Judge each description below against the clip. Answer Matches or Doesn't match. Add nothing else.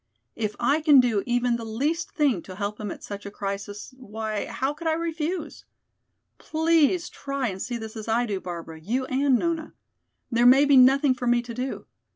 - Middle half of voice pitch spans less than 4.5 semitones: Doesn't match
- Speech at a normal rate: Matches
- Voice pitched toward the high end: Matches